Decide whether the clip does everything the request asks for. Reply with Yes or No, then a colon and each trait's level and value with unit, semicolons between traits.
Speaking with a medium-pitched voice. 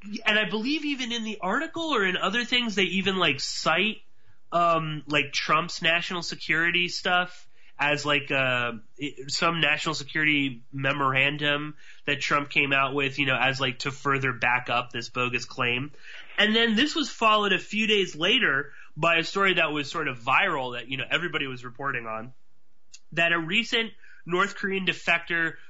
Yes: medium, 160 Hz